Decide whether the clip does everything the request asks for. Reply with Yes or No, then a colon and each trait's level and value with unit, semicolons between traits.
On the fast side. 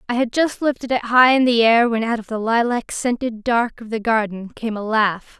Yes: fast, 245 wpm